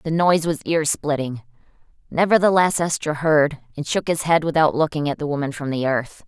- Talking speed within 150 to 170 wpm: No, average, 190 wpm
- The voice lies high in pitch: No, medium, 150 Hz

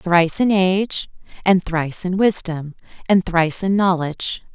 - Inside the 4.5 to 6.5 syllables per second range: Yes, 4.8 syllables/s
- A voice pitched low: No, medium, 180 Hz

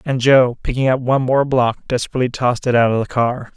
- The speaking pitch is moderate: No, low, 125 Hz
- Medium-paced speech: No, fast, 235 wpm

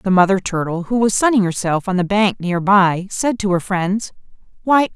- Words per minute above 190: Yes, fast, 205 wpm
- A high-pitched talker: Yes, high, 195 Hz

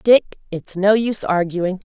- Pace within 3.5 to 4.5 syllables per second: Yes, 4.2 syllables/s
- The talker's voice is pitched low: No, high, 195 Hz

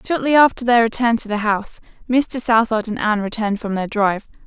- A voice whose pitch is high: Yes, high, 225 Hz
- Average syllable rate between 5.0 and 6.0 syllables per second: No, 6.2 syllables/s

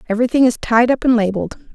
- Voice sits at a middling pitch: No, high, 235 Hz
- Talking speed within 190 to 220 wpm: Yes, fast, 205 wpm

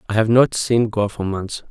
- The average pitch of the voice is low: Yes, low, 110 Hz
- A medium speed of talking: No, fast, 245 wpm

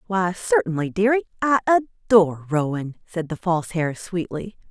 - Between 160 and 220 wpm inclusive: No, average, 140 wpm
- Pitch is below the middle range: No, medium, 185 Hz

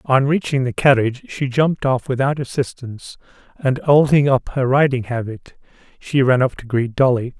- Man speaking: Yes, male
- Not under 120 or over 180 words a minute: Yes, average, 170 wpm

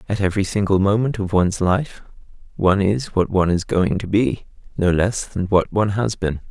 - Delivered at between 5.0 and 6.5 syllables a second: Yes, 5.5 syllables/s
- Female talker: No, male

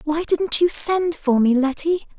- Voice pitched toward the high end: Yes, very high, 310 Hz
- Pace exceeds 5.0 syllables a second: No, 4.1 syllables/s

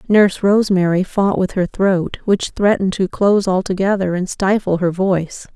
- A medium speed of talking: Yes, average, 160 wpm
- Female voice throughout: Yes, female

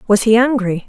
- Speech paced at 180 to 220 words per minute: Yes, fast, 205 wpm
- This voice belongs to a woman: Yes, female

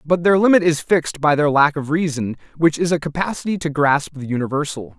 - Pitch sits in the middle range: Yes, medium, 155 Hz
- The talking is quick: Yes, fast, 215 wpm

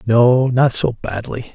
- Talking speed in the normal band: Yes, average, 155 wpm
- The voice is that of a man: Yes, male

